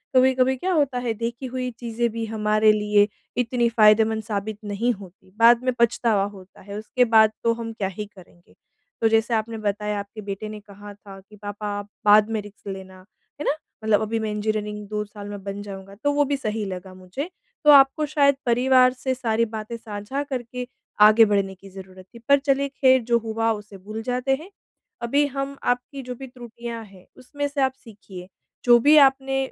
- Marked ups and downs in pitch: No, average, 3.6 semitones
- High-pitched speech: Yes, high, 225 Hz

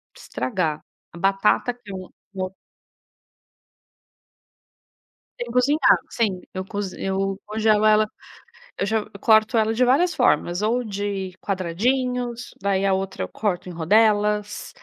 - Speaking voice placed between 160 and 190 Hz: No, high, 210 Hz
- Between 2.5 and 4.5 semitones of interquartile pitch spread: Yes, average, 2.8 semitones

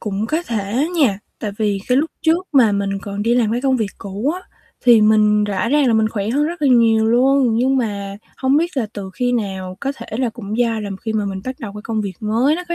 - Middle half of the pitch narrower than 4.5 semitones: Yes, average, 4.1 semitones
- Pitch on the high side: Yes, high, 225 Hz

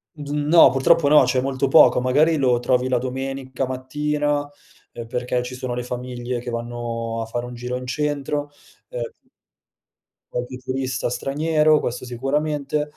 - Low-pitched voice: Yes, low, 130 Hz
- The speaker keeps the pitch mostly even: No, average, 3.0 semitones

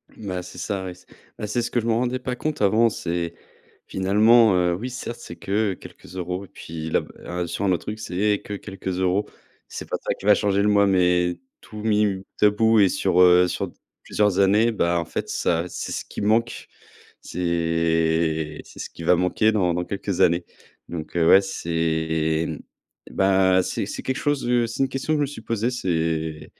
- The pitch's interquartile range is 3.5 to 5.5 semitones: Yes, average, 3.9 semitones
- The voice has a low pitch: Yes, very low, 95 Hz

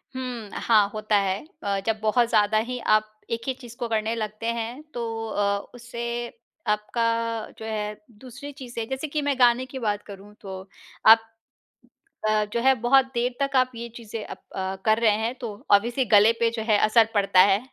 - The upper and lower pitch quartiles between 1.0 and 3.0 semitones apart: Yes, narrow, 2.4 semitones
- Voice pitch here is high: Yes, high, 225 Hz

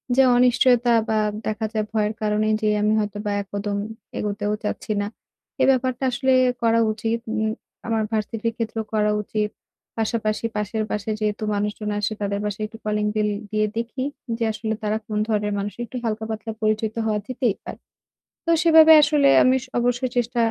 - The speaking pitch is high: Yes, high, 220 Hz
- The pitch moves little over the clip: Yes, narrow, 1.8 semitones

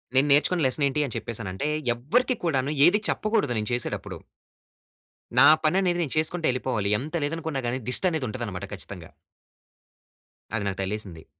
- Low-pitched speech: Yes, low, 130 Hz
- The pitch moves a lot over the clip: Yes, wide, 6.8 semitones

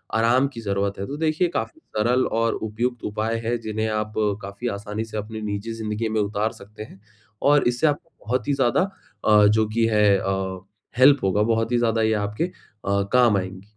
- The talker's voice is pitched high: No, low, 110 Hz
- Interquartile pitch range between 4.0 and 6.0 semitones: No, average, 2.8 semitones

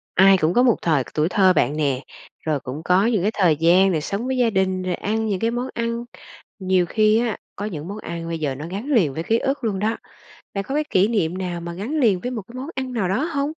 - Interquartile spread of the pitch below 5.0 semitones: No, average, 5.3 semitones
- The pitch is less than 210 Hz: Yes, high, 195 Hz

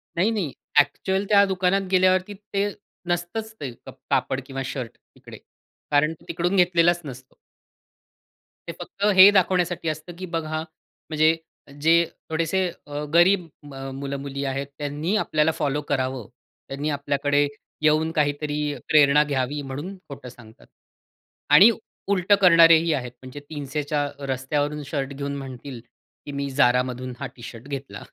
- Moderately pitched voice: Yes, medium, 150 Hz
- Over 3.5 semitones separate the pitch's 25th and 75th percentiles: Yes, average, 4.0 semitones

